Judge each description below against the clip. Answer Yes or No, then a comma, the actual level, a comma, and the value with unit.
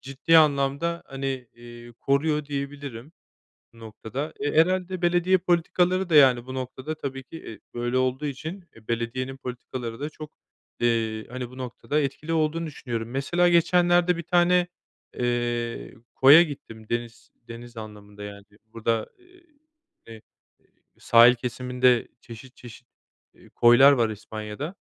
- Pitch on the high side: No, low, 130 Hz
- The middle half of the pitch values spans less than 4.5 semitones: No, average, 5.0 semitones